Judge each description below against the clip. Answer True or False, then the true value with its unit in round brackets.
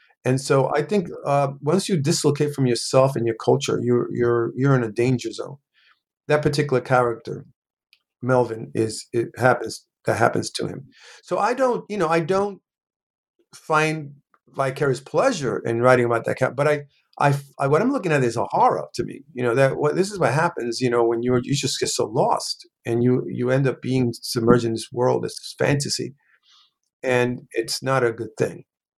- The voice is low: True (130 Hz)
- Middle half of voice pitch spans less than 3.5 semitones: False (3.8 semitones)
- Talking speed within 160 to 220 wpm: True (195 wpm)